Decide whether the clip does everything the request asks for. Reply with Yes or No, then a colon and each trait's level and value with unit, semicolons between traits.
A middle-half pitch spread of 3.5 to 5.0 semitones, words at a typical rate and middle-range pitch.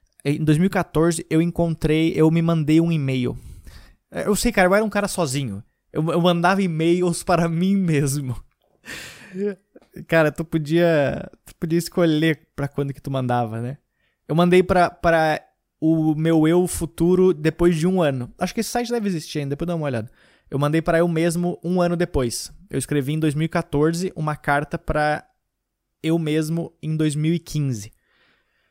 No: narrow, 2.6 semitones; average, 160 wpm; medium, 165 Hz